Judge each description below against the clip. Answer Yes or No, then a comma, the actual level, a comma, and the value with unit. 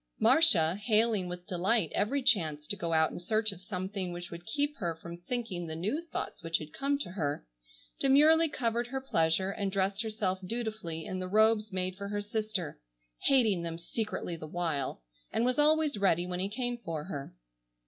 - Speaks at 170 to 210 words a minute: Yes, average, 190 wpm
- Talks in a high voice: Yes, high, 195 Hz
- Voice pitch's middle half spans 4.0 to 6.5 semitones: Yes, average, 5.1 semitones